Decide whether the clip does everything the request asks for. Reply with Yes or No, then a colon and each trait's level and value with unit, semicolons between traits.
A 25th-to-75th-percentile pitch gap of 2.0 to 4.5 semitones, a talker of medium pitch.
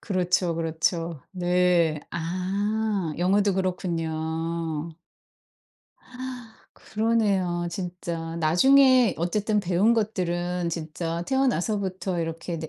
Yes: average, 3.3 semitones; medium, 180 Hz